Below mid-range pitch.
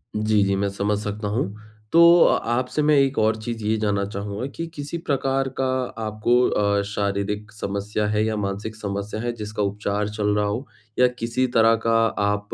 Yes: low, 105 Hz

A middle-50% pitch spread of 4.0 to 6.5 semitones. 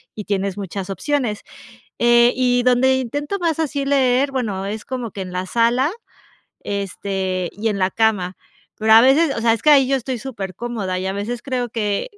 Yes: average, 4.8 semitones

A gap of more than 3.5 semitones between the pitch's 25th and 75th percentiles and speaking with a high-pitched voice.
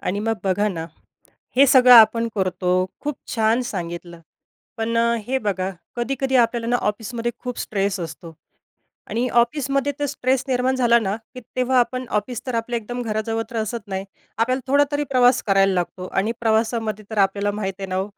Yes: average, 3.9 semitones; high, 230 Hz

